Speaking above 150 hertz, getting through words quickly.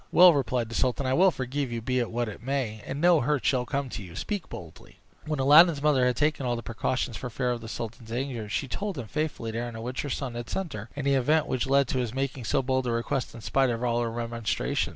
No: low, 125 Hz; fast, 270 wpm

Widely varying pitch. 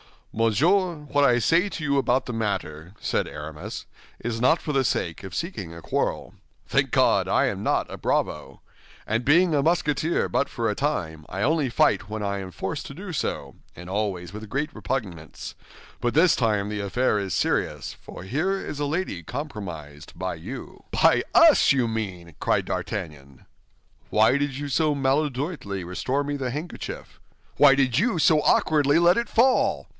Yes: wide, 7.1 semitones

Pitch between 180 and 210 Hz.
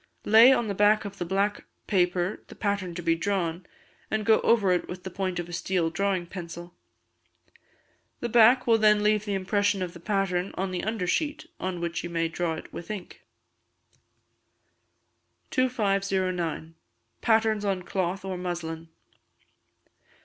Yes: high, 190 Hz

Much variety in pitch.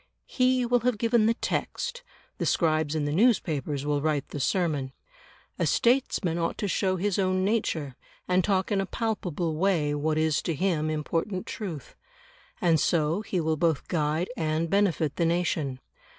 No: average, 4.4 semitones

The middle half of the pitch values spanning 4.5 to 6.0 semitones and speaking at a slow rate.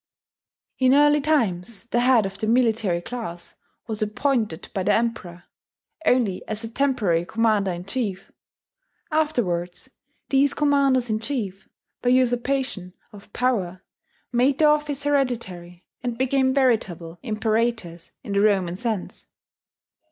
Yes: wide, 5.4 semitones; slow, 125 wpm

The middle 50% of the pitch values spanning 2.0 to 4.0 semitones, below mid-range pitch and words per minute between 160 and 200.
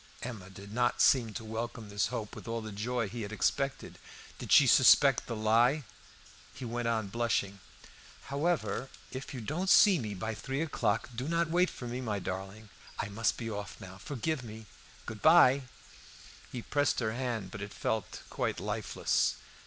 Yes: average, 3.6 semitones; low, 115 Hz; average, 175 wpm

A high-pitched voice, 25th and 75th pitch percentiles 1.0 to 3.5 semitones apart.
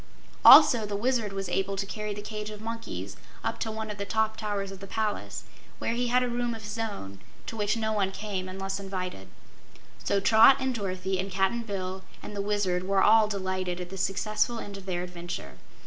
Yes: high, 205 Hz; narrow, 2.5 semitones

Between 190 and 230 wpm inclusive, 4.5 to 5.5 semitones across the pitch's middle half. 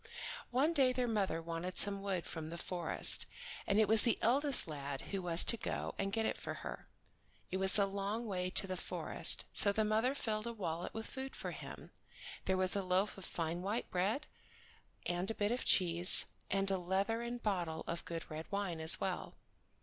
No: average, 200 wpm; average, 4.0 semitones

